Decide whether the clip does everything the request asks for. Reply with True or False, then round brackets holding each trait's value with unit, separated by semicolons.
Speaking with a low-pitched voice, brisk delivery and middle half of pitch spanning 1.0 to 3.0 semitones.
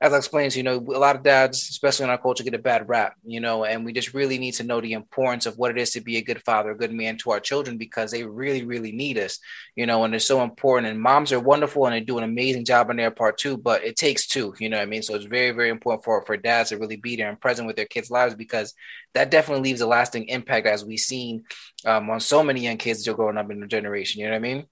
True (120 Hz; 300 wpm; 2.5 semitones)